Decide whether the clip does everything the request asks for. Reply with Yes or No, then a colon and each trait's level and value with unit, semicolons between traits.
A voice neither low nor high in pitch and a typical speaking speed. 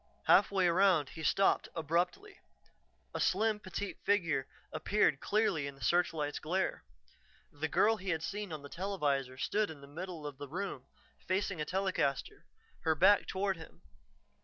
Yes: medium, 175 Hz; average, 155 wpm